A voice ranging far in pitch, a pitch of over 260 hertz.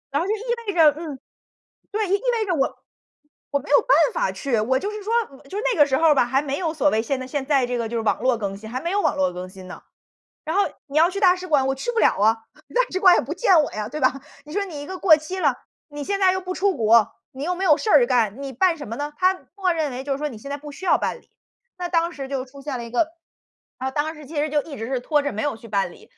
Yes: wide, 5.8 semitones; very high, 290 Hz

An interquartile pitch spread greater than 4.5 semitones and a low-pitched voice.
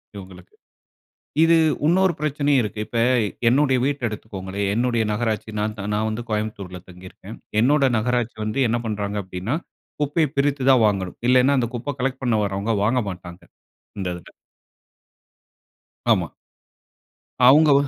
Yes: average, 5.1 semitones; low, 115 Hz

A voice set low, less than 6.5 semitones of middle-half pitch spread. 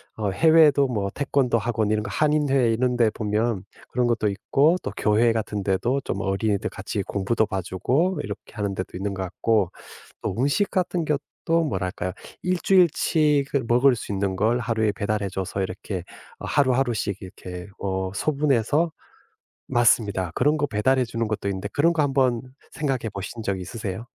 Yes: low, 115 Hz; wide, 5.5 semitones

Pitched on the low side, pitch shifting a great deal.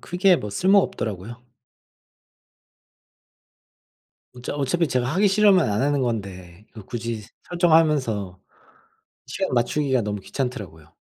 Yes: low, 125 Hz; wide, 7.8 semitones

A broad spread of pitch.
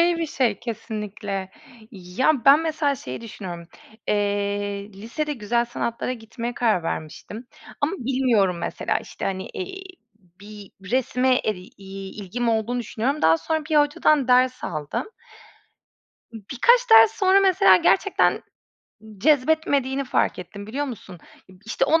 Yes: wide, 6.1 semitones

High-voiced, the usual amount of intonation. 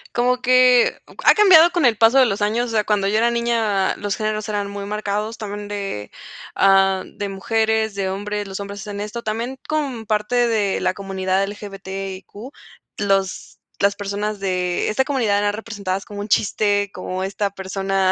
No: high, 205 Hz; narrow, 2.2 semitones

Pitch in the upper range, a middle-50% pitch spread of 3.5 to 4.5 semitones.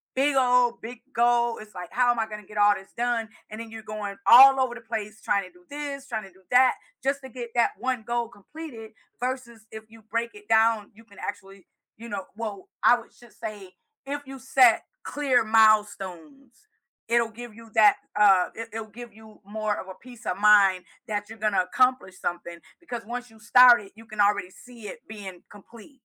No: high, 225 Hz; average, 2.9 semitones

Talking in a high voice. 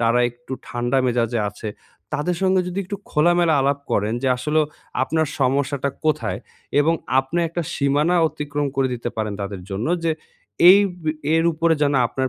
No: medium, 140 Hz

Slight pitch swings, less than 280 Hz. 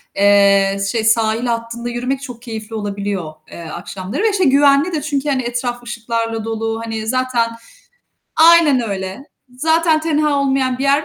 No: average, 4.1 semitones; high, 240 Hz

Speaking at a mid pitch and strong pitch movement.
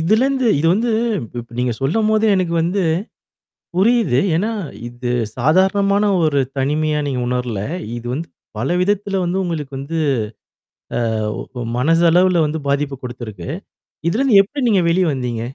Yes: medium, 165 Hz; wide, 7.3 semitones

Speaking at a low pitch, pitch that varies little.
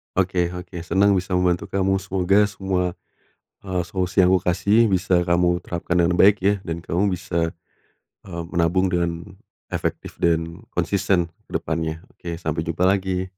Yes: very low, 90 Hz; narrow, 2.0 semitones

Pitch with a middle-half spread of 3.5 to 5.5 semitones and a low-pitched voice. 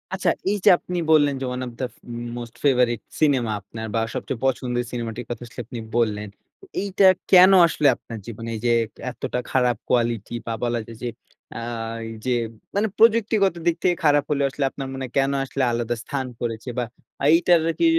Yes: average, 4.2 semitones; low, 125 Hz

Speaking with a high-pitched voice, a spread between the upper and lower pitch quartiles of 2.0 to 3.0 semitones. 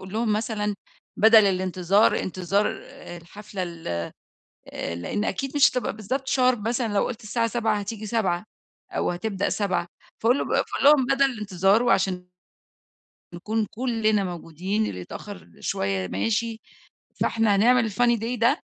No: high, 210 Hz; average, 3.7 semitones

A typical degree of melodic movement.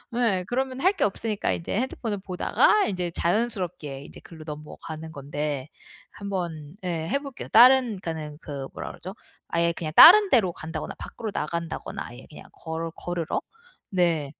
No: wide, 5.9 semitones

